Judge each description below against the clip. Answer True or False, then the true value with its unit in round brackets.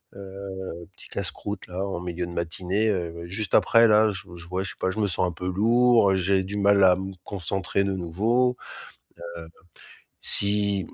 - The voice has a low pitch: True (95 Hz)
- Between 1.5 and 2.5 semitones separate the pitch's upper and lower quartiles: True (2.2 semitones)